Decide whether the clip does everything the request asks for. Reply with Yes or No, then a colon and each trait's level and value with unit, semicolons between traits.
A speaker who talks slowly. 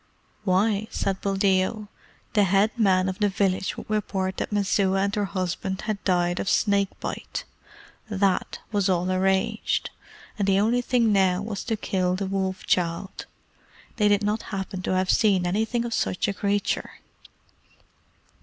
No: average, 155 wpm